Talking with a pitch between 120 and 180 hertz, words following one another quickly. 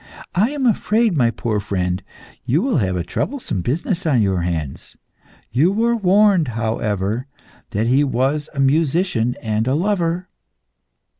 No: low, 135 Hz; average, 145 wpm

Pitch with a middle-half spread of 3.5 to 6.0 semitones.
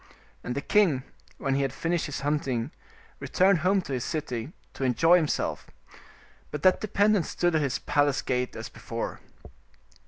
Yes: average, 4.7 semitones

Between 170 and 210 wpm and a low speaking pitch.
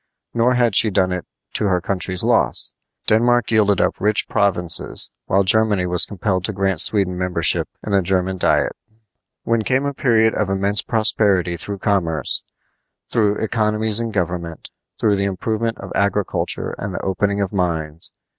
No: average, 160 wpm; low, 100 Hz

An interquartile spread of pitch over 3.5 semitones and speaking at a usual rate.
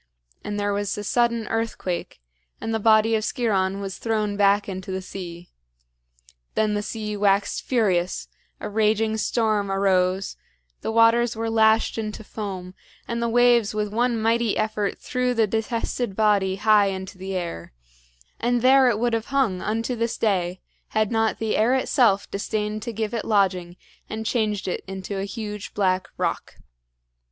No: narrow, 2.5 semitones; average, 165 wpm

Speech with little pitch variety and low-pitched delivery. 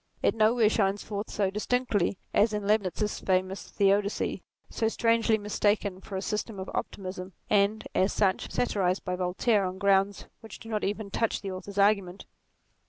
No: narrow, 2.0 semitones; high, 200 Hz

